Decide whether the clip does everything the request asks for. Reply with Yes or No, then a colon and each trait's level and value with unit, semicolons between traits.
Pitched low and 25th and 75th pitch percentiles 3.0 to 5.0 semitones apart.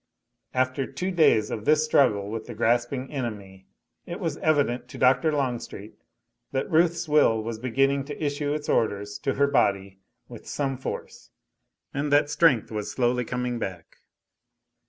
Yes: low, 130 Hz; average, 4.6 semitones